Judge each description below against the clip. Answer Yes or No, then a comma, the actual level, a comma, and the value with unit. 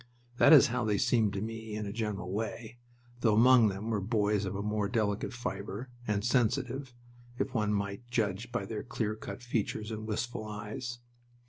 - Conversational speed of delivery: Yes, average, 185 wpm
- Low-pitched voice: Yes, low, 110 Hz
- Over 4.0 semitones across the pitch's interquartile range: No, narrow, 2.5 semitones